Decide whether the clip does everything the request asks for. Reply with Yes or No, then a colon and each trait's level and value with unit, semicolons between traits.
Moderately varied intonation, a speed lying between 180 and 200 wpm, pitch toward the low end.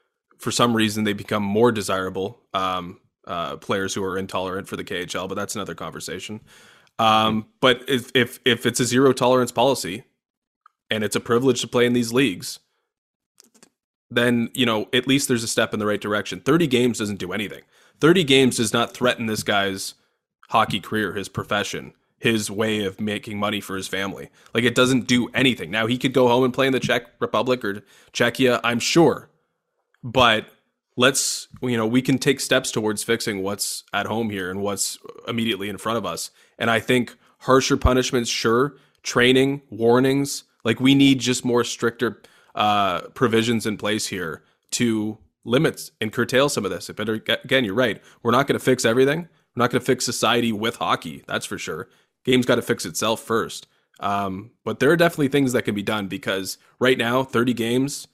Yes: average, 3.2 semitones; average, 190 wpm; low, 120 Hz